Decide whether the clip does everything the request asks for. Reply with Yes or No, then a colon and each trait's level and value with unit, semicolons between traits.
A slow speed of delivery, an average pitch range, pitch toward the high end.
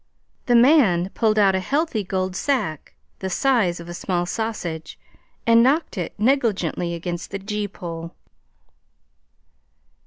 Yes: slow, 130 wpm; average, 4.9 semitones; high, 195 Hz